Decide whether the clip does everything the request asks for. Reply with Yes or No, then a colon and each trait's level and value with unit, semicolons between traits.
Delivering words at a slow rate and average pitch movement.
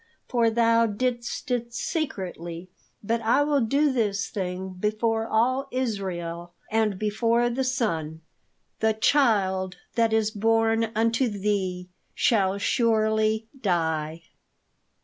Yes: slow, 110 wpm; average, 3.6 semitones